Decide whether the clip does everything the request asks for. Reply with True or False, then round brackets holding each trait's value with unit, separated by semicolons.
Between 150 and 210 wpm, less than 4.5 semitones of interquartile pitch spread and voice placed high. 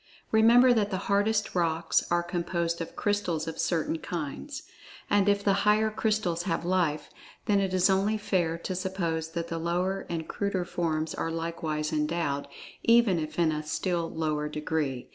False (165 wpm; 3.7 semitones; 175 Hz)